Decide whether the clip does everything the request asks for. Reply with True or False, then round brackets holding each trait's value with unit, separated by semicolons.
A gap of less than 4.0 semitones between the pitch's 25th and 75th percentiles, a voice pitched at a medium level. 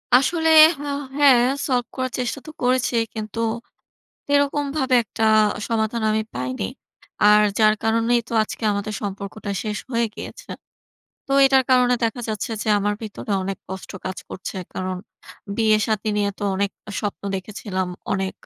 False (3.6 semitones; 220 Hz)